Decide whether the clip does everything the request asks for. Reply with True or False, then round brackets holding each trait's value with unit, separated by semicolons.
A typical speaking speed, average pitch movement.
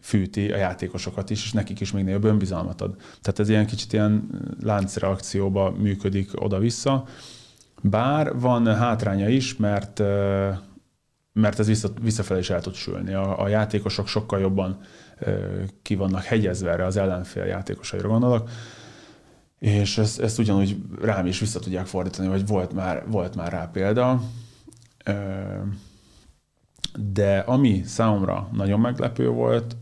False (135 wpm; 2.2 semitones)